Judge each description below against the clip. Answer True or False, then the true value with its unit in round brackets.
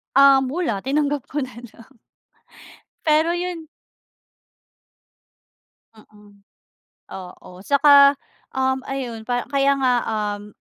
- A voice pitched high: True (265 Hz)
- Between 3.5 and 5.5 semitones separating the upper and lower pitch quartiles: True (4.3 semitones)